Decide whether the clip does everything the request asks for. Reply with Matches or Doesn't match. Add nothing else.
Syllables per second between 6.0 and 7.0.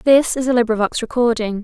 Matches